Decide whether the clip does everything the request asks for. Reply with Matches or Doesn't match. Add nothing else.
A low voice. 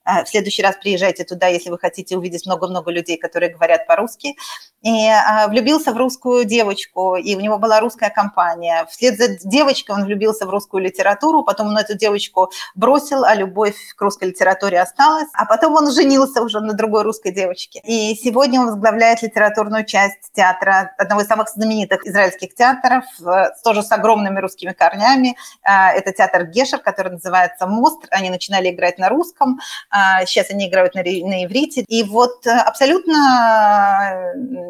Doesn't match